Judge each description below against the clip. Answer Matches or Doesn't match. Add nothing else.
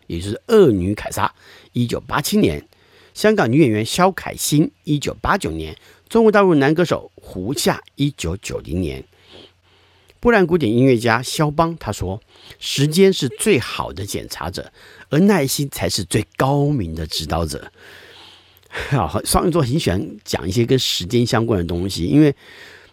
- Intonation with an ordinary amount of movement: Doesn't match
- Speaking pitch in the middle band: Doesn't match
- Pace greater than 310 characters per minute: Doesn't match